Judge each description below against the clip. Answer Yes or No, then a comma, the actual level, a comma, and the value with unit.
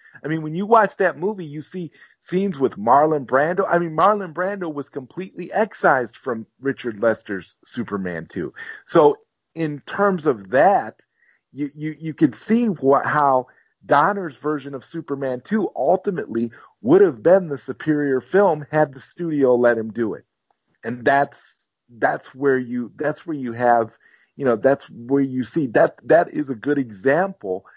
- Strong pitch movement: Yes, wide, 5.7 semitones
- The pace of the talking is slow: No, average, 165 wpm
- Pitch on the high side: No, medium, 145 Hz